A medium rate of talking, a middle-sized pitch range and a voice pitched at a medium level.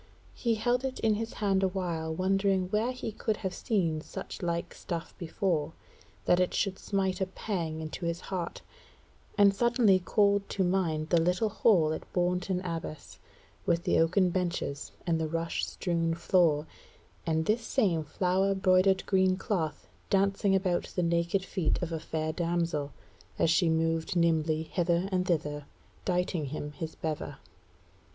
Yes: average, 160 wpm; average, 3.0 semitones; medium, 180 Hz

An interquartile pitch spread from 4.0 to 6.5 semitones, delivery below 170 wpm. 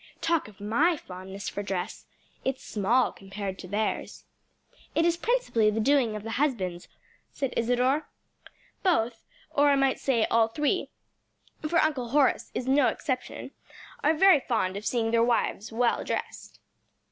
Yes: average, 5.3 semitones; average, 150 wpm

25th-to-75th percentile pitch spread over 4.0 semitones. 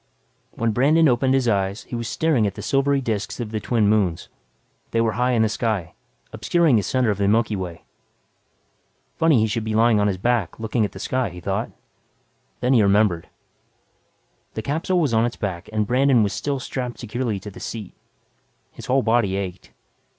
No: average, 3.7 semitones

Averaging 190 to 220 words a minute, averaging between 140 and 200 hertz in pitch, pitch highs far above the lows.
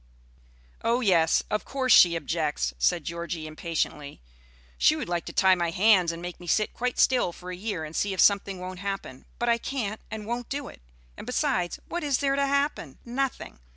Yes: average, 200 wpm; high, 190 Hz; wide, 6.2 semitones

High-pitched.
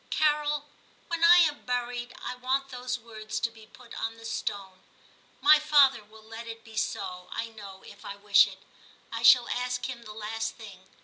Yes: high, 230 Hz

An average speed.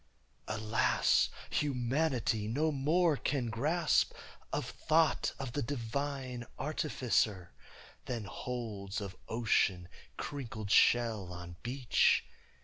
No: slow, 95 wpm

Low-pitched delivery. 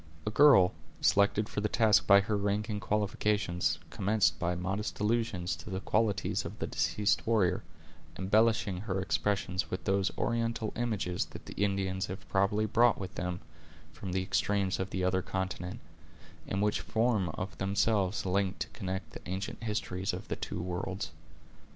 Yes: low, 100 Hz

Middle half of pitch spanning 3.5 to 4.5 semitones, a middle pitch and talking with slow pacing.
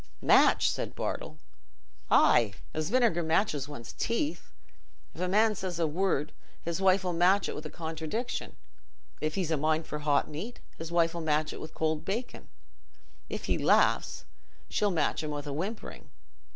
No: average, 4.0 semitones; medium, 165 Hz; average, 165 wpm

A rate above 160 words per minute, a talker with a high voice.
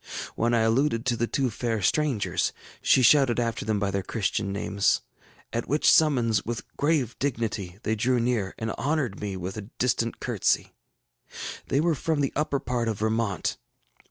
No: average, 170 wpm; low, 115 Hz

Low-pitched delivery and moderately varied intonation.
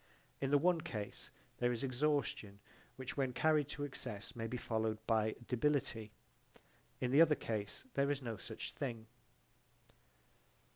Yes: low, 125 Hz; average, 4.3 semitones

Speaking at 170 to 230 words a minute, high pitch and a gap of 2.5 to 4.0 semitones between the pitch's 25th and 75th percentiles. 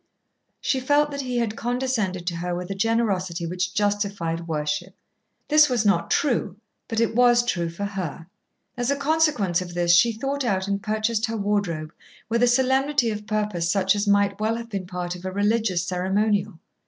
No: average, 185 wpm; high, 205 Hz; average, 4.7 semitones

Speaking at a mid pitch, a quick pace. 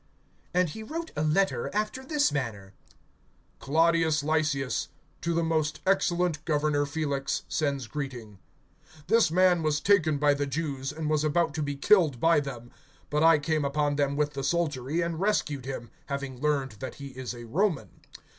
No: medium, 150 Hz; average, 165 wpm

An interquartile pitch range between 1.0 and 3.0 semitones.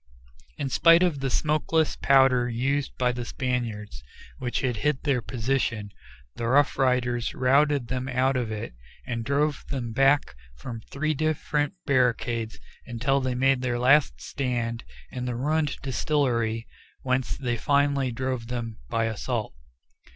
Yes: average, 2.7 semitones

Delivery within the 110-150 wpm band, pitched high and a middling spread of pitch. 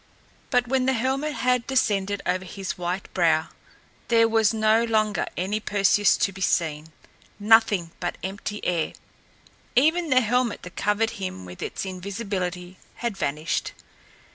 Yes: average, 140 wpm; high, 205 Hz; average, 4.1 semitones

